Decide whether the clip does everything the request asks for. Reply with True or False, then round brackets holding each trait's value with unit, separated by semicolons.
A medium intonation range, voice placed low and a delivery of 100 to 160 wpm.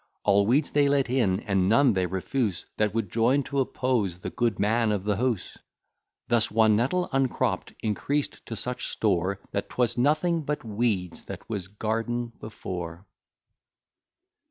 True (4.3 semitones; 115 Hz; 155 wpm)